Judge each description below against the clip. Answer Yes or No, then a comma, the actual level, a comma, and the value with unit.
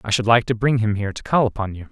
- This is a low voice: Yes, low, 110 Hz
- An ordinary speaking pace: No, fast, 345 wpm